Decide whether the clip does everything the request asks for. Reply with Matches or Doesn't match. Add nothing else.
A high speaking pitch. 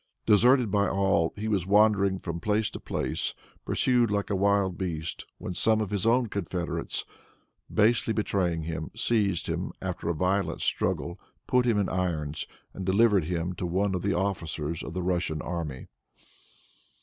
Doesn't match